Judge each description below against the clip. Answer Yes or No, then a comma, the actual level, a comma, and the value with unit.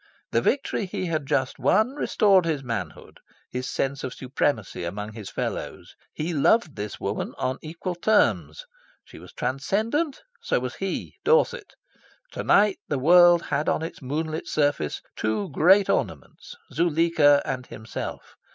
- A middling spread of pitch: No, wide, 6.3 semitones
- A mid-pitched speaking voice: Yes, medium, 155 Hz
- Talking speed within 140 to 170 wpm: Yes, average, 145 wpm